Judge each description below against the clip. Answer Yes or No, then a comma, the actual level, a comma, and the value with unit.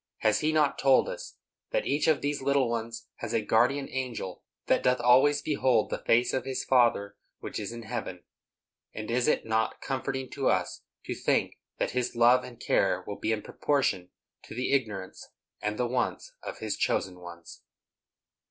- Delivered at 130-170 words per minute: No, average, 180 wpm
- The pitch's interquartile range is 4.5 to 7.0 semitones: No, average, 3.7 semitones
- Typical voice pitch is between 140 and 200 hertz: No, low, 125 Hz